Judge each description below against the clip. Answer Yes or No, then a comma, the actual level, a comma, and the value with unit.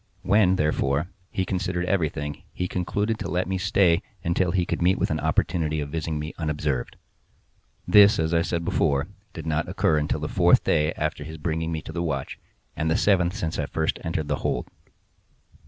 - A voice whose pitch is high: No, very low, 80 Hz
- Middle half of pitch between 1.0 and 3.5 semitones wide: Yes, average, 2.8 semitones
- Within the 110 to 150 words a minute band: No, average, 190 wpm